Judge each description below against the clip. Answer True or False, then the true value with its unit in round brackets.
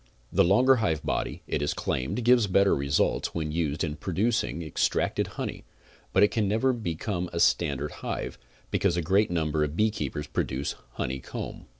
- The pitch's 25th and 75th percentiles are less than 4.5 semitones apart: False (5.6 semitones)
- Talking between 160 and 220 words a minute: True (170 wpm)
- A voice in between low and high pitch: False (85 Hz)